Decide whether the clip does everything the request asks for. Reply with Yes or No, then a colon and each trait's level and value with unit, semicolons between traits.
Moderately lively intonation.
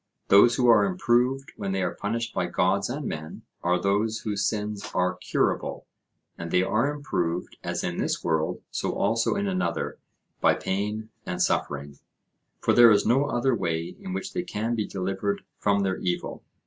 Yes: average, 4.6 semitones